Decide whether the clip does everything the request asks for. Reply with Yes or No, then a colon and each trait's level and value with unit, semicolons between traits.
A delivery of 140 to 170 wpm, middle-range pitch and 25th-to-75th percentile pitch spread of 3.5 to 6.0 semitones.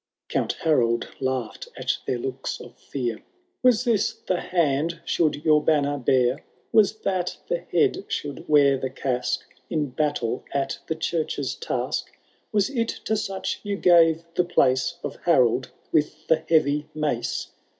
Yes: average, 155 wpm; medium, 150 Hz; average, 4.8 semitones